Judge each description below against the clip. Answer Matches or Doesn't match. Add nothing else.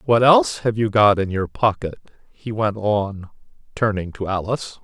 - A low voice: Matches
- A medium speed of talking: Matches